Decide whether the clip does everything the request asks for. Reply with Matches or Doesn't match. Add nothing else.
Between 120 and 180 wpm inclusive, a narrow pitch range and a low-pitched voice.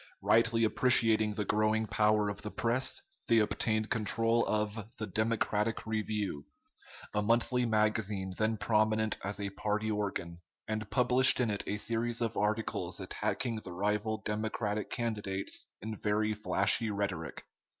Matches